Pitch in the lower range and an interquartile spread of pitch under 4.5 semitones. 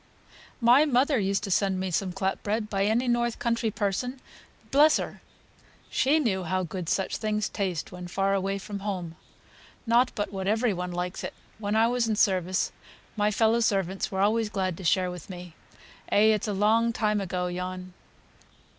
No: high, 200 Hz; average, 3.3 semitones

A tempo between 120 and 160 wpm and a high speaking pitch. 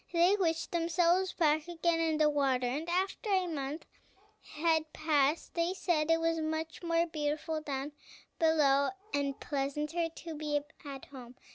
Yes: average, 150 wpm; very high, 315 Hz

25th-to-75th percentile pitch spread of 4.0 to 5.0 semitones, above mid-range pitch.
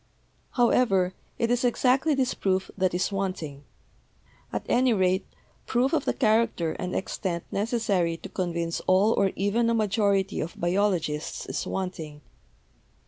Yes: average, 4.4 semitones; high, 195 Hz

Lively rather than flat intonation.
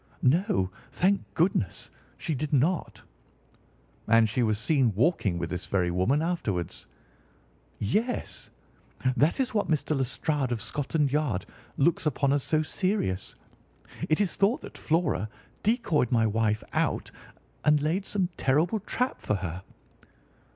Yes: wide, 7.9 semitones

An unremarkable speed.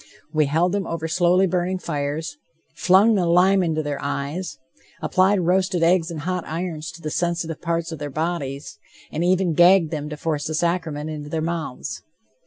Yes: average, 175 wpm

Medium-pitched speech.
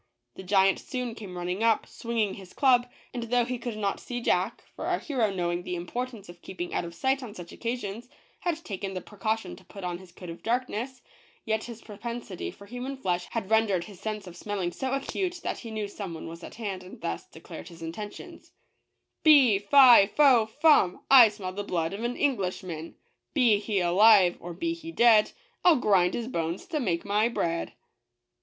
No: high, 210 Hz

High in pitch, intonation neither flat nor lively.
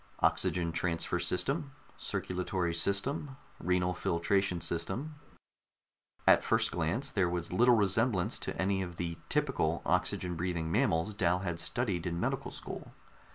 No: very low, 90 Hz; average, 3.8 semitones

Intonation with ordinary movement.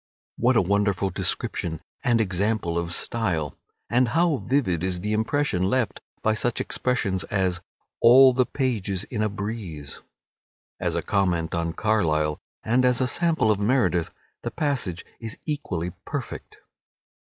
No: wide, 5.7 semitones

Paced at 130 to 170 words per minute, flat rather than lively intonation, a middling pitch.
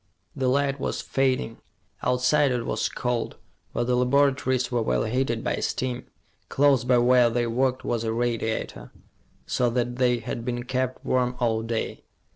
No: average, 160 wpm; narrow, 1.6 semitones; low, 125 Hz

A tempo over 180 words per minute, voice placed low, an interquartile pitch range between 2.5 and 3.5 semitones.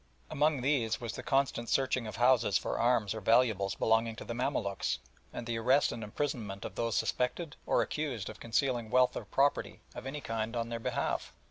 Yes: average, 195 wpm; low, 120 Hz; average, 2.8 semitones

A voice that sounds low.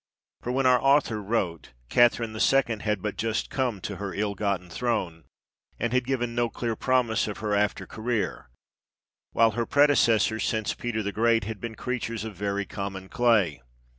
Yes: low, 110 Hz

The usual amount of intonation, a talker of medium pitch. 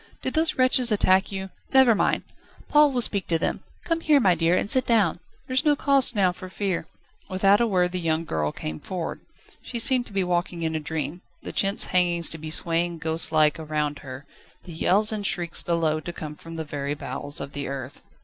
Yes: average, 5.0 semitones; medium, 175 Hz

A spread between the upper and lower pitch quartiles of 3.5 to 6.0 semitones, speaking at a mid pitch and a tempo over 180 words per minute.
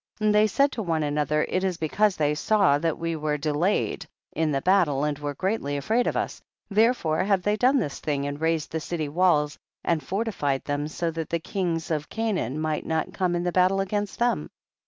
Yes: average, 4.8 semitones; medium, 165 Hz; fast, 205 wpm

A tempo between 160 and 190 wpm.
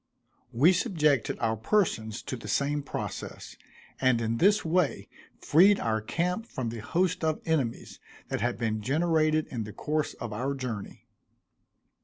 No: average, 150 wpm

